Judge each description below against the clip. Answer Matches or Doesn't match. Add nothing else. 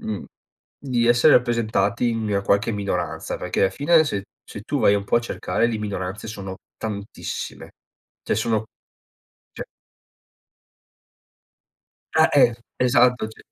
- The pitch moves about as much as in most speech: Matches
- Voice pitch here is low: Matches